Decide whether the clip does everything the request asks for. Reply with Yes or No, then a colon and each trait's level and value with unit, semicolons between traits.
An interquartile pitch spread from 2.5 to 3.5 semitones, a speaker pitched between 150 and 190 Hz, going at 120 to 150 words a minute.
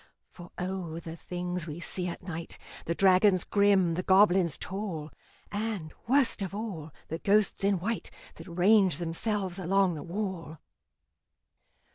Yes: average, 3.0 semitones; medium, 185 Hz; average, 140 wpm